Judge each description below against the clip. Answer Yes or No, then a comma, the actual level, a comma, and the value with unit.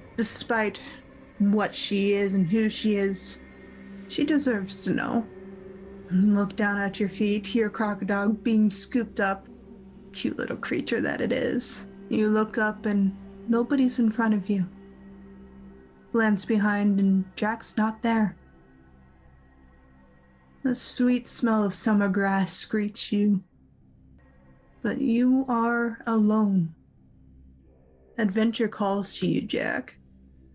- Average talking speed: No, slow, 120 wpm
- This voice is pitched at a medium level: No, high, 200 Hz